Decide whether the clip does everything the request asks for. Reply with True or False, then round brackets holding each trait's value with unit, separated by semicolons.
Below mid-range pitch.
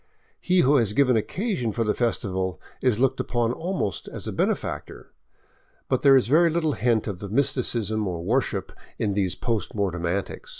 True (115 Hz)